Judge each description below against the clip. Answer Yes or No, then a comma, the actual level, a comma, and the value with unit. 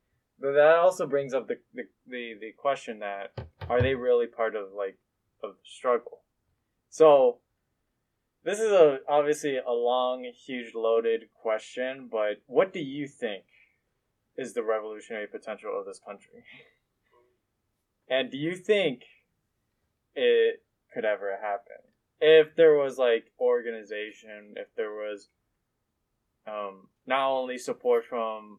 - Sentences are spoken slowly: Yes, slow, 130 wpm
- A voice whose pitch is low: Yes, low, 125 Hz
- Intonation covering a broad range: Yes, wide, 7.1 semitones